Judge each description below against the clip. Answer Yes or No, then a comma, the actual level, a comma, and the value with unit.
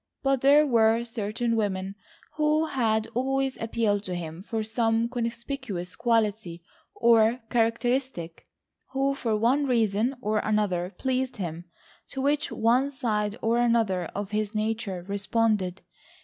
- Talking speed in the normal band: No, slow, 130 wpm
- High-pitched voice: Yes, high, 225 Hz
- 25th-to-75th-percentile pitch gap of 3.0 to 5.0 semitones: Yes, average, 3.4 semitones